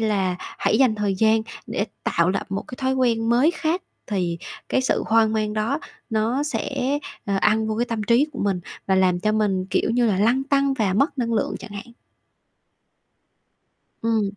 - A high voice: Yes, high, 220 Hz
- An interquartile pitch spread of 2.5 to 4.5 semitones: Yes, average, 3.9 semitones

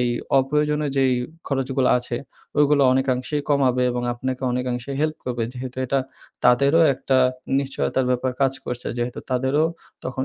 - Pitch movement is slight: Yes, narrow, 1.9 semitones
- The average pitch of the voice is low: Yes, low, 130 Hz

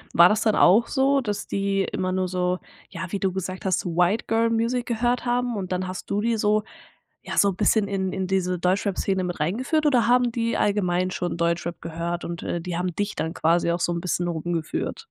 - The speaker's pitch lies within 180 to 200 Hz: Yes, high, 190 Hz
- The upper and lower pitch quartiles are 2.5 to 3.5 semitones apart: No, average, 3.9 semitones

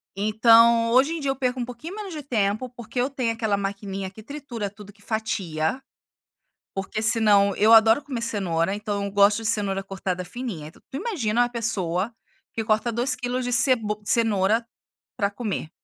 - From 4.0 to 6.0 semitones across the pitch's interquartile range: No, average, 3.5 semitones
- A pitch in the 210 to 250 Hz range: Yes, high, 225 Hz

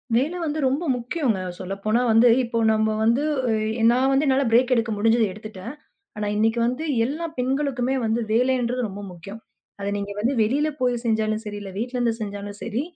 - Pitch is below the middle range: No, high, 235 Hz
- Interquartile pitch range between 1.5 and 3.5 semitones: Yes, average, 3.2 semitones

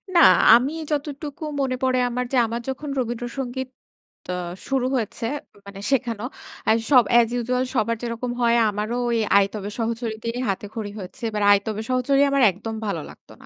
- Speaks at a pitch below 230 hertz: No, high, 235 Hz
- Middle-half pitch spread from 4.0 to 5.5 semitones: No, average, 2.9 semitones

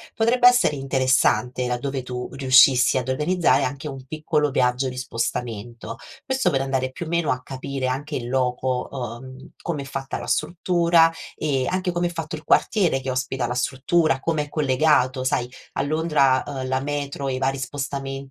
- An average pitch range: Yes, average, 3.0 semitones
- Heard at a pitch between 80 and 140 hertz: Yes, low, 135 Hz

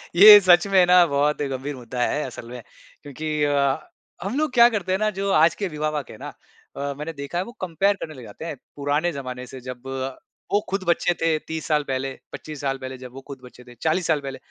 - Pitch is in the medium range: Yes, medium, 150 Hz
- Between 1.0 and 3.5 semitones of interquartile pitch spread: No, average, 4.6 semitones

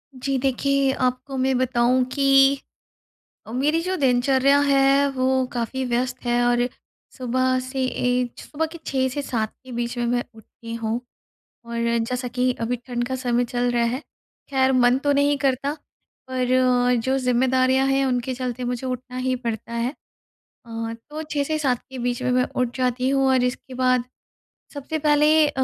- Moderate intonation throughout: No, narrow, 1.7 semitones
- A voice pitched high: Yes, very high, 255 Hz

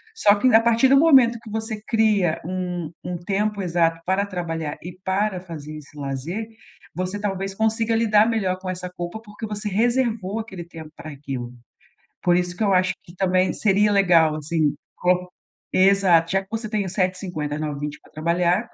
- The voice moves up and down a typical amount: Yes, average, 3.8 semitones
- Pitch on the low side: No, medium, 185 Hz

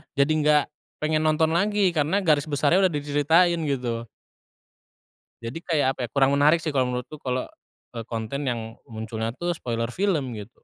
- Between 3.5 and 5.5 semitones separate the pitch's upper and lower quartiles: Yes, average, 4.6 semitones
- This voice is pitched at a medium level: Yes, medium, 145 Hz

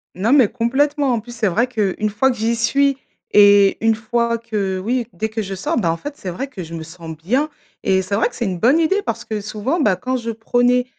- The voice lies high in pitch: Yes, high, 225 Hz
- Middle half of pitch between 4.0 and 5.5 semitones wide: Yes, average, 4.3 semitones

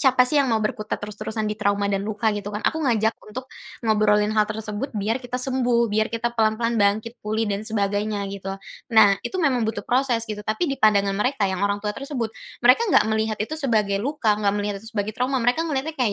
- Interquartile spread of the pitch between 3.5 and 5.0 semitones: No, average, 3.1 semitones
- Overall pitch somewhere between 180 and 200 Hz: No, high, 220 Hz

